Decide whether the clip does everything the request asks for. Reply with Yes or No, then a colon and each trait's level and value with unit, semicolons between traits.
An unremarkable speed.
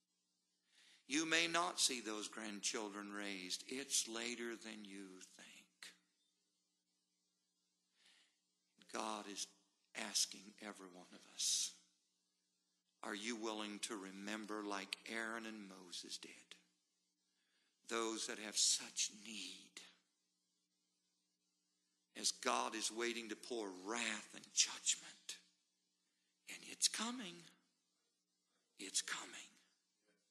No: slow, 95 wpm